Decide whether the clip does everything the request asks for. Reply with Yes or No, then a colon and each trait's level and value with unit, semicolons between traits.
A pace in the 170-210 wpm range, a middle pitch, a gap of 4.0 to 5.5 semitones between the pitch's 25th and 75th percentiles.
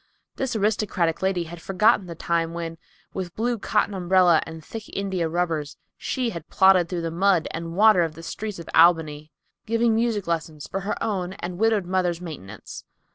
No: average, 180 wpm; medium, 180 Hz; average, 3.5 semitones